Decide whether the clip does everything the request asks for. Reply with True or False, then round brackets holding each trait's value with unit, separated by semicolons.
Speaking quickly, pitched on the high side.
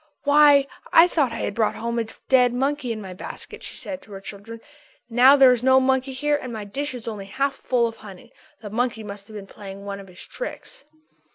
True (225 wpm; 240 Hz)